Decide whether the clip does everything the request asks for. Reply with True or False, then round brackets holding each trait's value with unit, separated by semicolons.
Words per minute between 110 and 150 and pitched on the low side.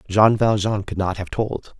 False (200 wpm; 100 Hz)